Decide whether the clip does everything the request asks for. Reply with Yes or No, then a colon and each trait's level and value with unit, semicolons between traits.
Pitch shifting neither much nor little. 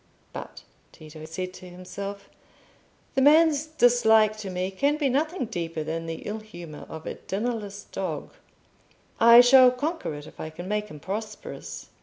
No: wide, 6.0 semitones